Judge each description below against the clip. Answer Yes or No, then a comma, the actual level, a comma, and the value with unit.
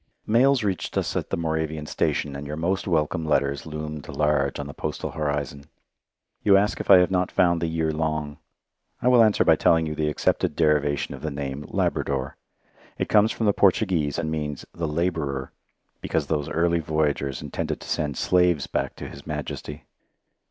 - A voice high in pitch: No, very low, 80 Hz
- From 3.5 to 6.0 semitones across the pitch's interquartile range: No, average, 3.0 semitones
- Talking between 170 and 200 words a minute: Yes, average, 180 wpm